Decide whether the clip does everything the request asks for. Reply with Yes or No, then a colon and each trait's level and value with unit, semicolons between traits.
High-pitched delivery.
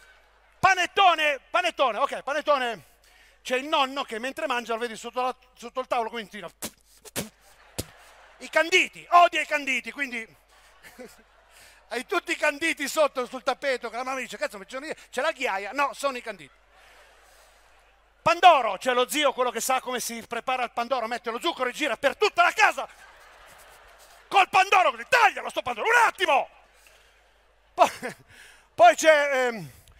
Yes: very high, 265 Hz